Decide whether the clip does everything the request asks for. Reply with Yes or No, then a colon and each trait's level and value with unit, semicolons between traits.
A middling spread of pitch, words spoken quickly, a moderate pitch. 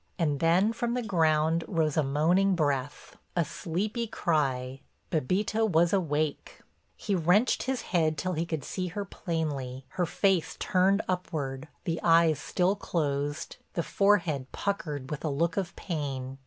No: average, 4.1 semitones; average, 145 wpm; medium, 165 Hz